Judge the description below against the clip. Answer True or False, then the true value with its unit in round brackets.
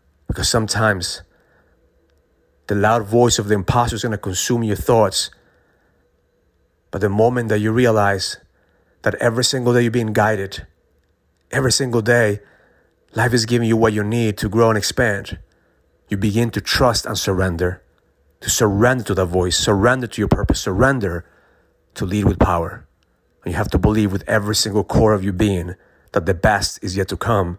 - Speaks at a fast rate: False (175 wpm)